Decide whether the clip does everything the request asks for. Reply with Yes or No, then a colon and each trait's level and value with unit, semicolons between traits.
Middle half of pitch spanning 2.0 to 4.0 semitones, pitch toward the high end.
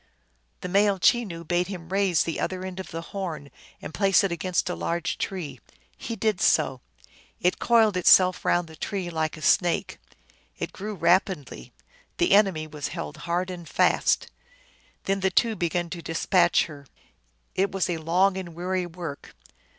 No: narrow, 2.6 semitones; medium, 180 Hz